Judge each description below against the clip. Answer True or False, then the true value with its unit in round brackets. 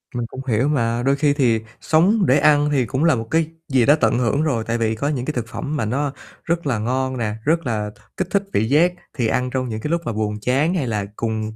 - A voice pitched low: True (130 Hz)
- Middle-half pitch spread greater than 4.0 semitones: True (4.7 semitones)